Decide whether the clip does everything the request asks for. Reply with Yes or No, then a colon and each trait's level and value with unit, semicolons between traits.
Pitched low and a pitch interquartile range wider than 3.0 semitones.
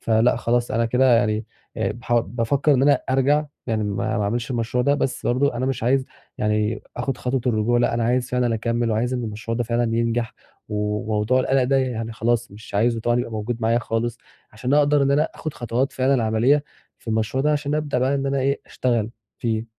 No: low, 120 Hz; average, 2.7 semitones